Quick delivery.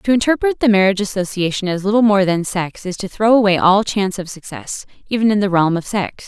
Yes: fast, 230 wpm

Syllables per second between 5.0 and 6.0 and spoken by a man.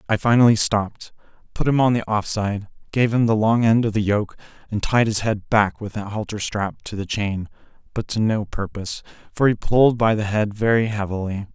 Yes: 5.3 syllables/s; male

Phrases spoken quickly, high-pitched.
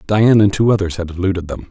No: fast, 245 wpm; low, 100 Hz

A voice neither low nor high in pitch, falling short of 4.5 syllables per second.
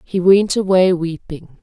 Yes: medium, 180 Hz; 4.0 syllables/s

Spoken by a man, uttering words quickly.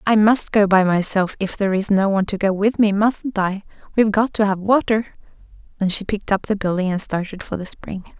No: female; fast, 235 wpm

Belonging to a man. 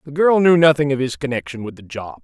Yes: male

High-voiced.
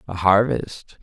No: low, 100 Hz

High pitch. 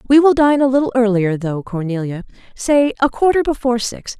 Yes: high, 240 Hz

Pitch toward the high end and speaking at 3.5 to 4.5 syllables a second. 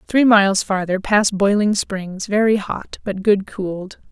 Yes: high, 200 Hz; 4.2 syllables/s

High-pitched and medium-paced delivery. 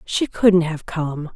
No: medium, 170 Hz; average, 180 wpm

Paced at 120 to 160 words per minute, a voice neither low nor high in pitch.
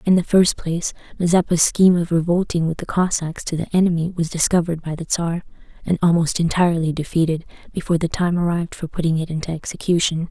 No: average, 185 wpm; medium, 170 Hz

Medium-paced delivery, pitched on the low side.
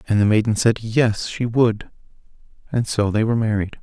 Yes: average, 190 wpm; low, 110 Hz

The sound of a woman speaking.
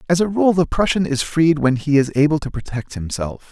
No: male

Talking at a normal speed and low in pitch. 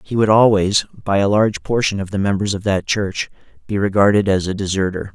No: fast, 210 wpm; low, 100 Hz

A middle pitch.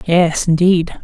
Yes: medium, 170 Hz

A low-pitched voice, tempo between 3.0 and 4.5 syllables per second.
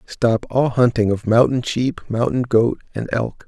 Yes: low, 120 Hz; 4.2 syllables/s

